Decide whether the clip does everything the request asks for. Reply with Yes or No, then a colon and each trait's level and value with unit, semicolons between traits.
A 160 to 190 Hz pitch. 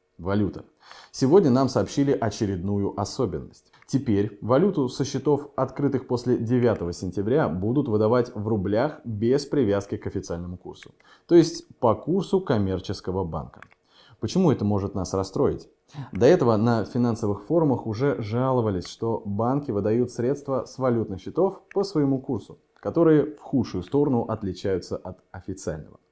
No: low, 115 Hz